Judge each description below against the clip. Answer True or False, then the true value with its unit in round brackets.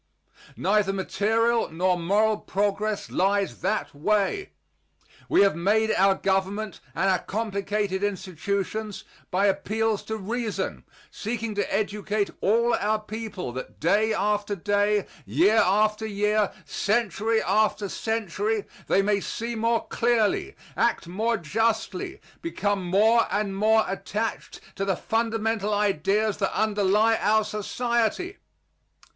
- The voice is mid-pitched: False (210 Hz)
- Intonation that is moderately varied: False (2.0 semitones)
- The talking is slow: True (120 wpm)